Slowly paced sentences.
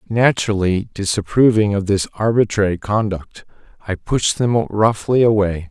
Yes: slow, 115 wpm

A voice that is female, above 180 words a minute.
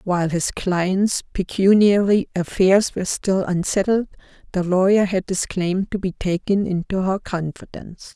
No: female; average, 140 wpm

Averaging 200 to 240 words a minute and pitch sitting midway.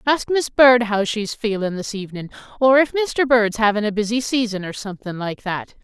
No: fast, 205 wpm; high, 225 Hz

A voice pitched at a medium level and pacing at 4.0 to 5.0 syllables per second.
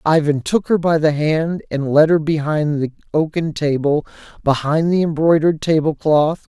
Yes: medium, 155 Hz; 4.7 syllables/s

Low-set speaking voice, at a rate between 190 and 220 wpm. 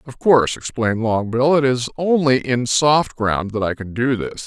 Yes: low, 125 Hz; average, 200 wpm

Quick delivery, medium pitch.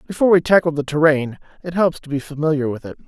Yes: fast, 235 wpm; medium, 155 Hz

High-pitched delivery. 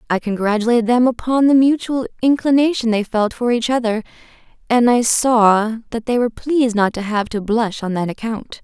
Yes: high, 235 Hz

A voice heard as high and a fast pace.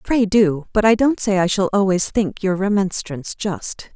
No: high, 195 Hz; average, 195 wpm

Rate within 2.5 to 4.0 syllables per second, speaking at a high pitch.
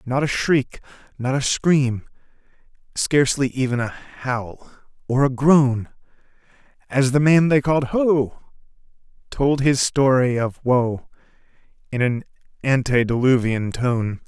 No: 3.9 syllables/s; low, 130 Hz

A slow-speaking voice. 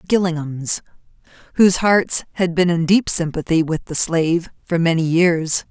No: average, 145 wpm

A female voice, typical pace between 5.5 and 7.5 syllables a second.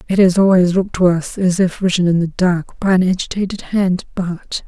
No: female; 5.3 syllables/s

